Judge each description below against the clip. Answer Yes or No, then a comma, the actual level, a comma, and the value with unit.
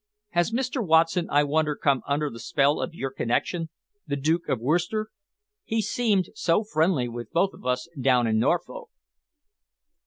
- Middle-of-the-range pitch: Yes, medium, 160 Hz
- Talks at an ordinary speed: Yes, average, 160 wpm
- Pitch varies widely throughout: Yes, wide, 5.7 semitones